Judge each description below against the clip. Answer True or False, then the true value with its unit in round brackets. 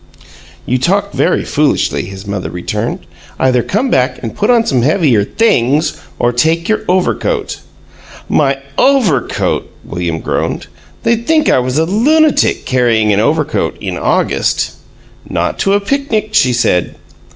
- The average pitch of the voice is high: False (150 Hz)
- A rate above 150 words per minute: False (140 wpm)